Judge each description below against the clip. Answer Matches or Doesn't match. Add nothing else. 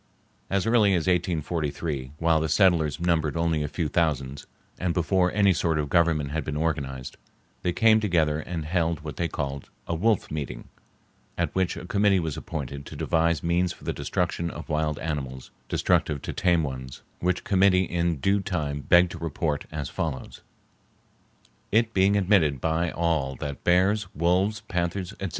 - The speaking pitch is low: Matches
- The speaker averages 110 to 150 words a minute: Doesn't match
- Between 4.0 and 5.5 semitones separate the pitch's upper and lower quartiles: Doesn't match